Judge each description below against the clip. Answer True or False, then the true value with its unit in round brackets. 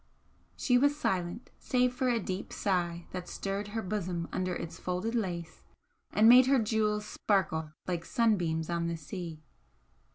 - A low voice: False (190 Hz)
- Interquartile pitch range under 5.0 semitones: True (4.6 semitones)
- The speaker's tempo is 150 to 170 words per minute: True (155 wpm)